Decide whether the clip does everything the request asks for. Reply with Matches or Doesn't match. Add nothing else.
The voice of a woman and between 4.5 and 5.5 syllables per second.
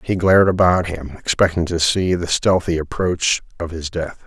Doesn't match